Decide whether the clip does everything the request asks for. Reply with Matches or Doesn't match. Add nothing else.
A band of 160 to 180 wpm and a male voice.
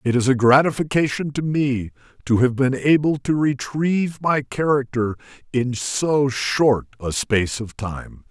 Doesn't match